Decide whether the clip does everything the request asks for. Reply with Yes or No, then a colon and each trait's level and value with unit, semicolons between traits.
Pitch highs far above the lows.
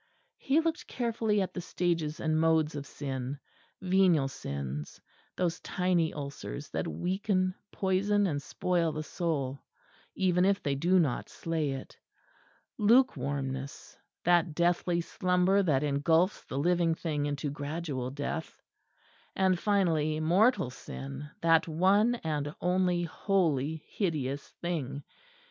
No: average, 4.3 semitones